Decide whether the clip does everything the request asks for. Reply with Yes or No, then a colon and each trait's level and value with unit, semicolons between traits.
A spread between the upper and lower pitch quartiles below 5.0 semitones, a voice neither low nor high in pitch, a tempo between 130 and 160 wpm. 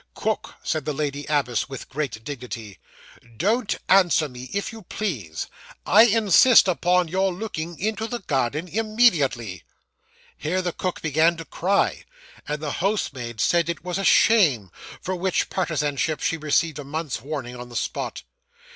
No: wide, 5.6 semitones; medium, 160 Hz; average, 155 wpm